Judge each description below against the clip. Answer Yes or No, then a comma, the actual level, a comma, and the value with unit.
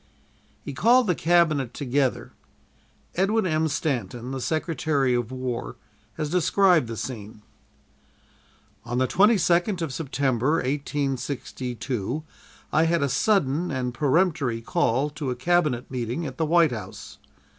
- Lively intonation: No, average, 4.9 semitones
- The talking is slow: Yes, slow, 125 wpm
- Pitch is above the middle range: No, medium, 140 Hz